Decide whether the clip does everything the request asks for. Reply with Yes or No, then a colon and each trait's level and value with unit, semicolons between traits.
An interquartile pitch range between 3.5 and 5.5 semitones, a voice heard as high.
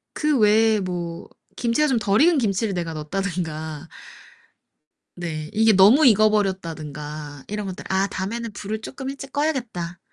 Yes: average, 5.2 semitones; high, 200 Hz